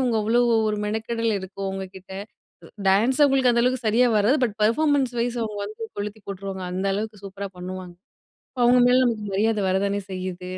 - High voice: Yes, high, 215 Hz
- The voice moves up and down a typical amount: Yes, average, 3.7 semitones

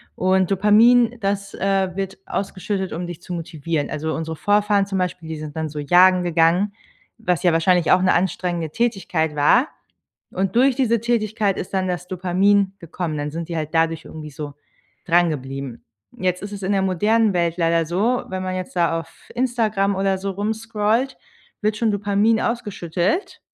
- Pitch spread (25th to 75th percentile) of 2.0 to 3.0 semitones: No, average, 3.8 semitones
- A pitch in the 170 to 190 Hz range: Yes, medium, 185 Hz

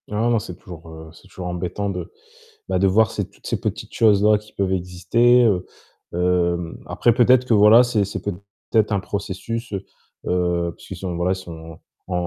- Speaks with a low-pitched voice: Yes, very low, 95 Hz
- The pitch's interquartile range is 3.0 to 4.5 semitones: Yes, average, 3.4 semitones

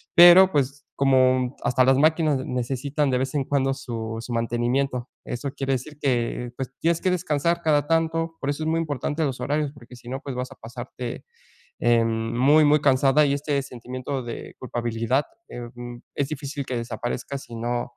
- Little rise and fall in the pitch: No, average, 3.2 semitones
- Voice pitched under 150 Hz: Yes, low, 135 Hz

